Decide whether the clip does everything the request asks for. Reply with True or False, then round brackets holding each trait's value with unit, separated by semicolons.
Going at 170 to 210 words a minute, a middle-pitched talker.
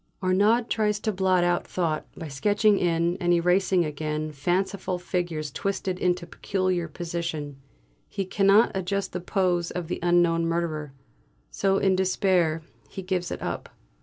False (150 wpm; 180 Hz)